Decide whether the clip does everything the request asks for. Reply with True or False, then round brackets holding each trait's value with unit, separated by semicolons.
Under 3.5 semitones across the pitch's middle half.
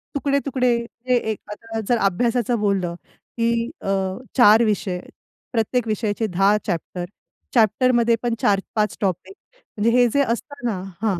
True (2.9 semitones)